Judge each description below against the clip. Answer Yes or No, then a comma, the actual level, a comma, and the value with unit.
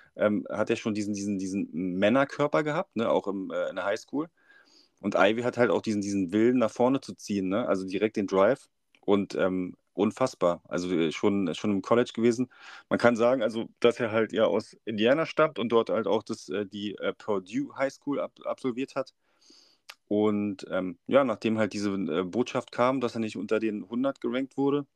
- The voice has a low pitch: Yes, low, 110 Hz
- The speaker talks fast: Yes, fast, 210 wpm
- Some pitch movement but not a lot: Yes, average, 3.6 semitones